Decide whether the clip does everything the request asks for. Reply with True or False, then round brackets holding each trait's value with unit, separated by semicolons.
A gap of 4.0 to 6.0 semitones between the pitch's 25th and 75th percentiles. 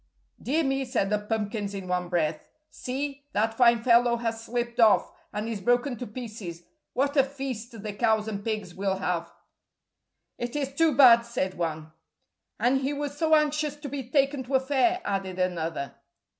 True (5.2 semitones)